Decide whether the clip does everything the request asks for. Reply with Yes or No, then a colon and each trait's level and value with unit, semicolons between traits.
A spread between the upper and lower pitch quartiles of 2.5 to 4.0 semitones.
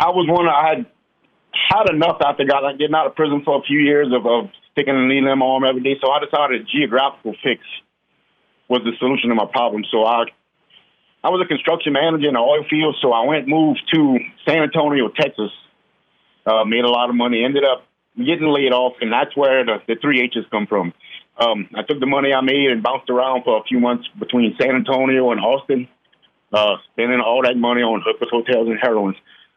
Yes: average, 3.6 semitones